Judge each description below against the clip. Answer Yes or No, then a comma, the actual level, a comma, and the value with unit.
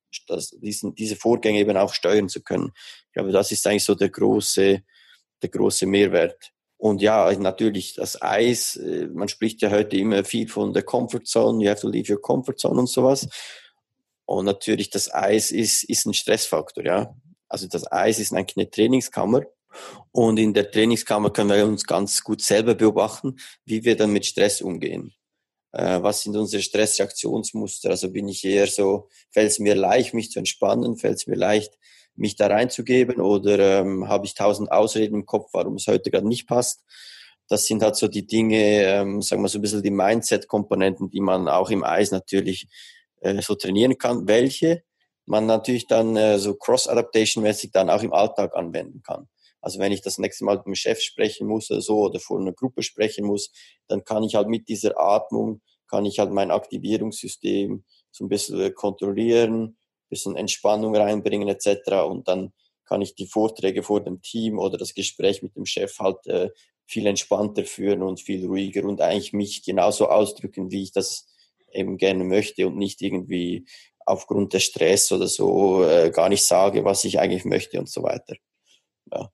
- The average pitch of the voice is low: Yes, low, 105 Hz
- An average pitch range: No, narrow, 2.0 semitones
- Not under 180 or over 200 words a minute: Yes, average, 185 wpm